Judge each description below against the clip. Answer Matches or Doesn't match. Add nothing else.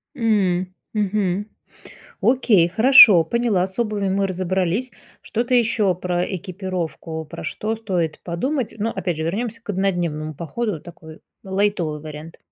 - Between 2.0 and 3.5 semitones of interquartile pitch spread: Doesn't match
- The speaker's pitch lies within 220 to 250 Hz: Doesn't match